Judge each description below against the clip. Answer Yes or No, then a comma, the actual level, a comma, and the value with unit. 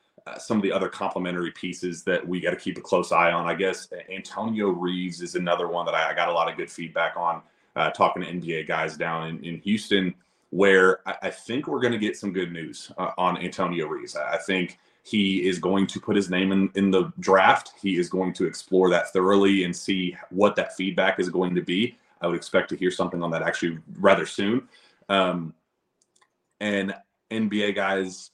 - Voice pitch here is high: No, very low, 90 Hz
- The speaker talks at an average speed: No, fast, 215 wpm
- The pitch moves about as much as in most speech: No, narrow, 1.9 semitones